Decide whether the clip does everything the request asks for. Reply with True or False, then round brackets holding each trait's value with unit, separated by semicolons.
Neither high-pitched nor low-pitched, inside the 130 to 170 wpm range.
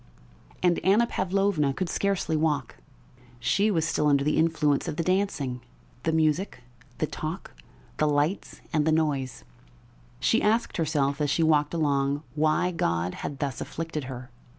True (155 Hz; 150 wpm)